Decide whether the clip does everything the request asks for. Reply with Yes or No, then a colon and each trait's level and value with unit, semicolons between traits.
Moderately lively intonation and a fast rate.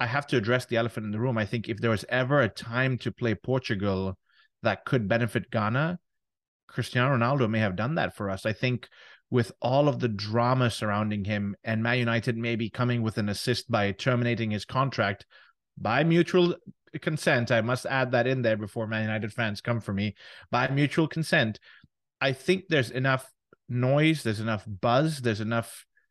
No: average, 3.1 semitones; average, 190 wpm